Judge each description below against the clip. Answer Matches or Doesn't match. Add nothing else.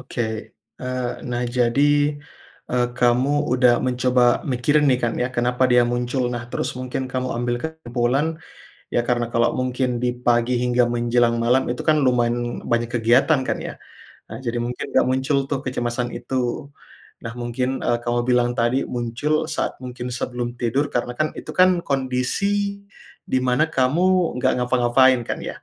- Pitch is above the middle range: Doesn't match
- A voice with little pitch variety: Matches